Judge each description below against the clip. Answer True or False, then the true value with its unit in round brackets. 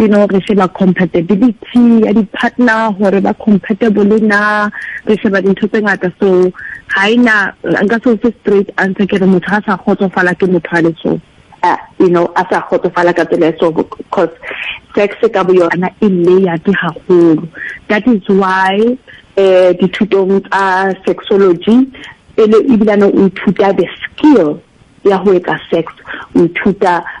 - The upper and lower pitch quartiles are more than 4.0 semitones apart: False (2.8 semitones)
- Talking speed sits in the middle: False (105 wpm)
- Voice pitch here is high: True (195 Hz)